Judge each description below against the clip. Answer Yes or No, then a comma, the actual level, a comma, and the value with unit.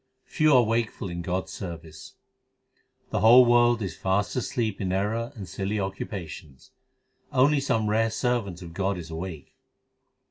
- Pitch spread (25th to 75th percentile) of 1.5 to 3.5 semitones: No, average, 4.4 semitones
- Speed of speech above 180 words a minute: No, average, 155 wpm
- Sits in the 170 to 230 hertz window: No, low, 100 Hz